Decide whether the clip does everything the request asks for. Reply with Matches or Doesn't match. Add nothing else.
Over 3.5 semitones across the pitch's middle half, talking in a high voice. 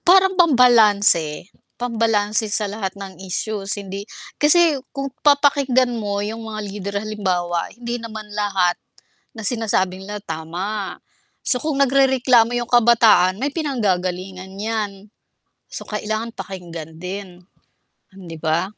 Matches